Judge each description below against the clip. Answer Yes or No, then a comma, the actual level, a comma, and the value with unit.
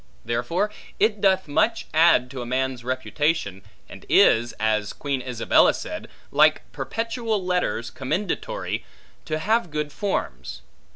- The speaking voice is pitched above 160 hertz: No, medium, 150 Hz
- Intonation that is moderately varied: No, wide, 8.3 semitones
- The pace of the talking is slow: Yes, slow, 125 wpm